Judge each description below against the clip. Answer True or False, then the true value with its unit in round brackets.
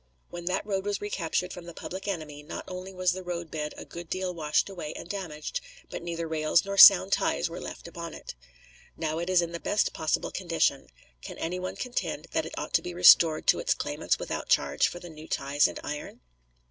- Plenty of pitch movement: False (2.7 semitones)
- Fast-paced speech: True (215 wpm)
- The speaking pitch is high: False (170 Hz)